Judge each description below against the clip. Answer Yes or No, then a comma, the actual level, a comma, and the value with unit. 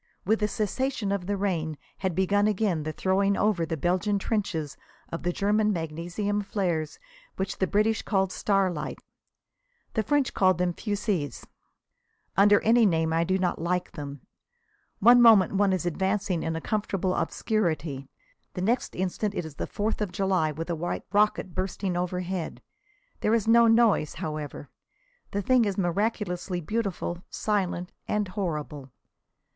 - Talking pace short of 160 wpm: Yes, average, 150 wpm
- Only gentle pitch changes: No, average, 3.4 semitones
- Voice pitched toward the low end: No, high, 190 Hz